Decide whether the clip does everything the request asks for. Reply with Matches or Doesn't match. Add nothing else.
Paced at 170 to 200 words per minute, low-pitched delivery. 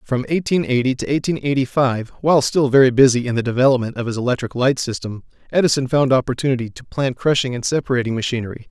Matches